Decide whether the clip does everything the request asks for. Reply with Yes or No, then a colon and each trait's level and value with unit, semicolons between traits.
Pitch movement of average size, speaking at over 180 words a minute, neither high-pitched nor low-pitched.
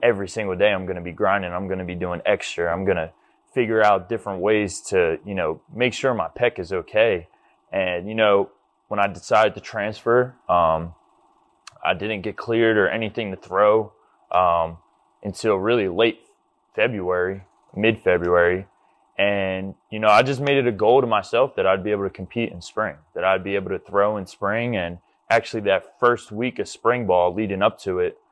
No: average, 3.6 semitones; average, 195 wpm; low, 100 Hz